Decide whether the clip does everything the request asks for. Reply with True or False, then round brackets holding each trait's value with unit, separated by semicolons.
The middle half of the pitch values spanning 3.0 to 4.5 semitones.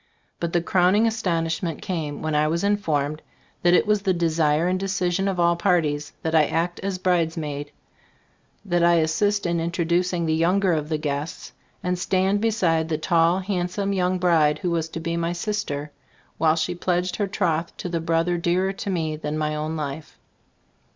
False (2.5 semitones)